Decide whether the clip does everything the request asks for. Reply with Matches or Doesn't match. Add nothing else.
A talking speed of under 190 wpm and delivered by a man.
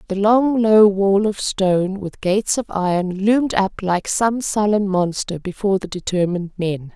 Doesn't match